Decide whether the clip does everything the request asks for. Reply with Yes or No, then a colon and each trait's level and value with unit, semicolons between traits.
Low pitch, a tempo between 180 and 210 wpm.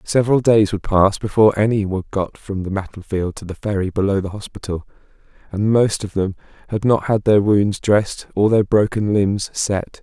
Yes: low, 100 Hz; average, 190 wpm